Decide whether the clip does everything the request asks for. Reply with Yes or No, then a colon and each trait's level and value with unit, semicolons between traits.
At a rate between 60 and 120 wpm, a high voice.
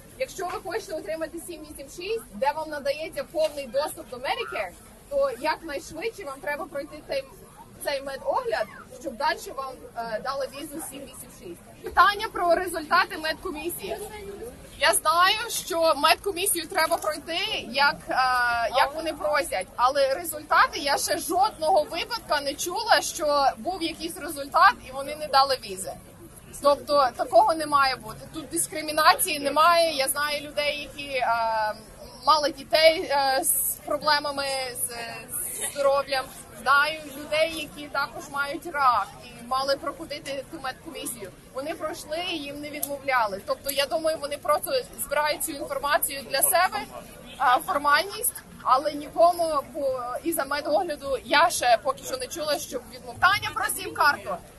No: average, 135 wpm; very high, 300 Hz